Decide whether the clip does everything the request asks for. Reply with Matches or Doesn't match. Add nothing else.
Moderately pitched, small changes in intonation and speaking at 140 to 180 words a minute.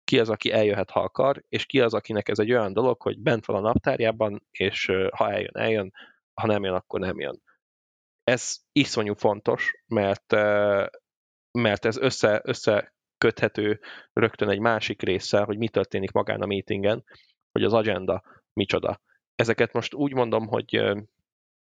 Doesn't match